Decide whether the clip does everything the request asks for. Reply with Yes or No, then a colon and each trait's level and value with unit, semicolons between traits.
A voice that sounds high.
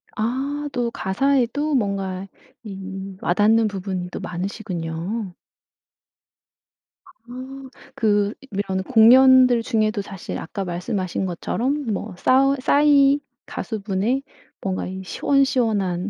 Yes: high, 215 Hz